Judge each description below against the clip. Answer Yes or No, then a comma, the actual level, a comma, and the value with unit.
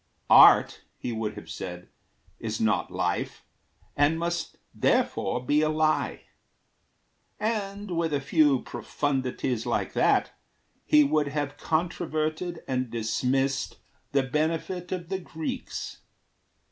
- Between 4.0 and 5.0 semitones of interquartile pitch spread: Yes, average, 4.3 semitones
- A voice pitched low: No, medium, 150 Hz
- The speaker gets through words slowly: Yes, slow, 115 wpm